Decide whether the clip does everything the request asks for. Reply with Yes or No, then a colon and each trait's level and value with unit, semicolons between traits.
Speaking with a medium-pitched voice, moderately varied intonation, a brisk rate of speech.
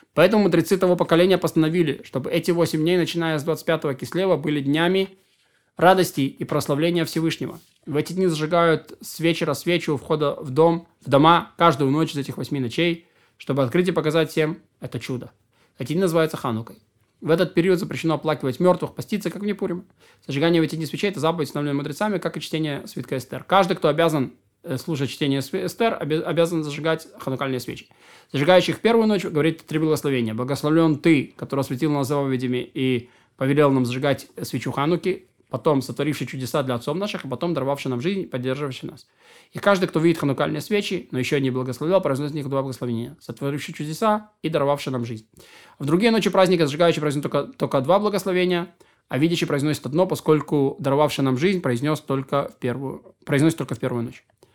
Yes: medium, 155 Hz; average, 3.9 semitones; fast, 175 wpm